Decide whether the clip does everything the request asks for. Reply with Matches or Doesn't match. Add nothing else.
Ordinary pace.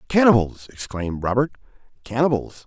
Doesn't match